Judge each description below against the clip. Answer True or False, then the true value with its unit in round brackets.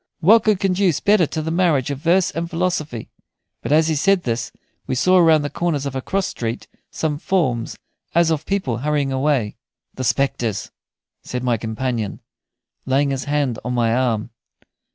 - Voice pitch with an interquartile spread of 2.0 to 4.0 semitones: False (5.5 semitones)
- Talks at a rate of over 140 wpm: True (175 wpm)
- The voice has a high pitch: False (145 Hz)